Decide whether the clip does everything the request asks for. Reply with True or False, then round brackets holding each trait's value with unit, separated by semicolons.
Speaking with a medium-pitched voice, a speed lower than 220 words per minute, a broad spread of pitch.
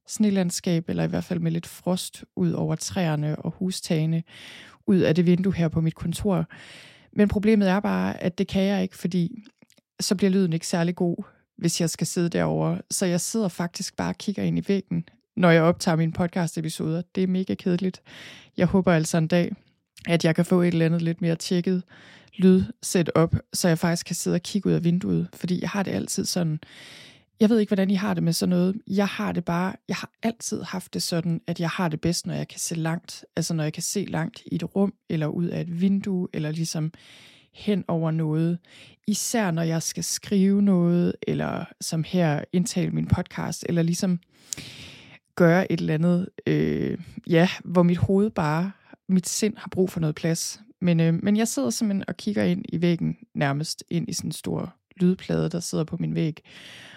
False (175 Hz; 210 wpm; 2.7 semitones)